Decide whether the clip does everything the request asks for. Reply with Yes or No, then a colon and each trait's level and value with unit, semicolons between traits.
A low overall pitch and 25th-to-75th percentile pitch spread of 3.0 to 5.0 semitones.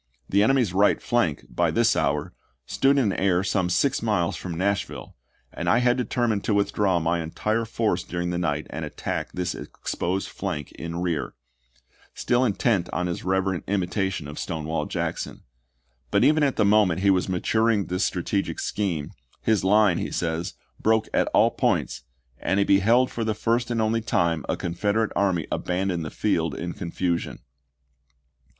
Yes: very low, 95 Hz; average, 4.2 semitones